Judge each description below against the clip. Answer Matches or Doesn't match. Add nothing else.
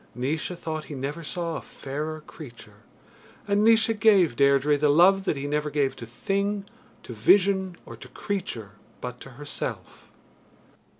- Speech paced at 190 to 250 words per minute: Doesn't match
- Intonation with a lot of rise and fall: Matches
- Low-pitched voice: Doesn't match